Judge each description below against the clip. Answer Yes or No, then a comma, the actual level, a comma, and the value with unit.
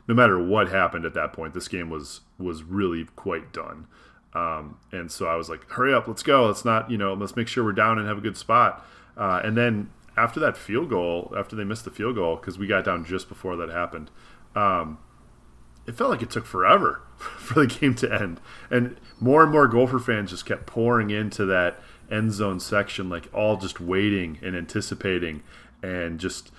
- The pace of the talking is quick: Yes, fast, 210 wpm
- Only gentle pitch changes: No, average, 4.3 semitones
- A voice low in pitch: Yes, low, 100 Hz